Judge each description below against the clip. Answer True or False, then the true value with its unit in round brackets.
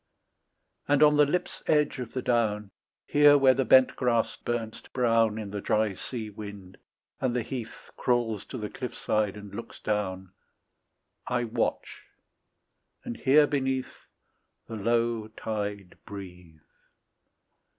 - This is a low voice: True (115 Hz)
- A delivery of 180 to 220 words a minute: False (140 wpm)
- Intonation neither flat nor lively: True (3.7 semitones)